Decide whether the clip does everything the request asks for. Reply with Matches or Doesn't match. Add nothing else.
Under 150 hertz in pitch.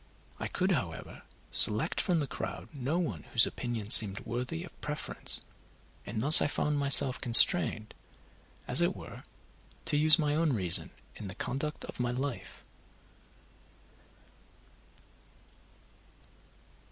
Matches